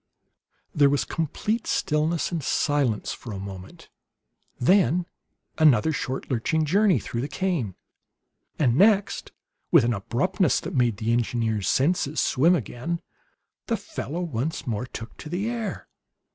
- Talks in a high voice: No, medium, 145 Hz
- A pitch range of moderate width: No, wide, 6.5 semitones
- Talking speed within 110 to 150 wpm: Yes, slow, 135 wpm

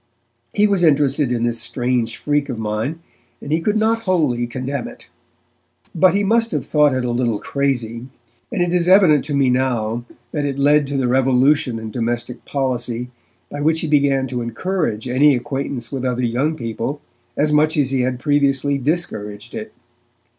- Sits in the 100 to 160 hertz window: Yes, low, 135 Hz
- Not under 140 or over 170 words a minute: No, average, 180 wpm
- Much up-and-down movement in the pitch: No, average, 3.8 semitones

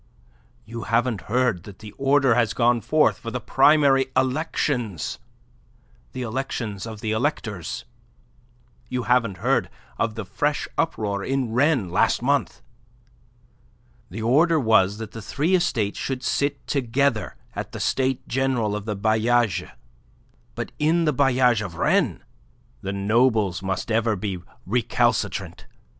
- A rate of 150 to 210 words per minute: No, slow, 135 wpm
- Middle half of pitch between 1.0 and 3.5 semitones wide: No, average, 4.0 semitones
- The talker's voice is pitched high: No, low, 120 Hz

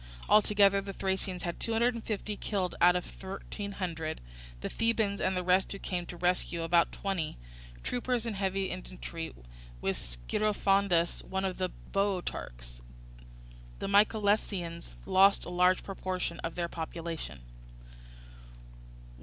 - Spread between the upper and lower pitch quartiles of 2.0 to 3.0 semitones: Yes, average, 2.7 semitones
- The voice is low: No, medium, 185 Hz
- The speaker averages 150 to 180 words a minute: No, slow, 135 wpm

